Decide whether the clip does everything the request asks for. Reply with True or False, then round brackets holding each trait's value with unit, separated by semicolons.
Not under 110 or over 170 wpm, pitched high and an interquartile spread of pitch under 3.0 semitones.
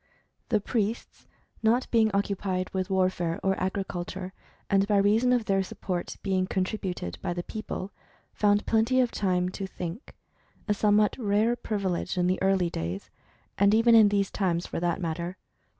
True (160 wpm; 195 Hz; 2.6 semitones)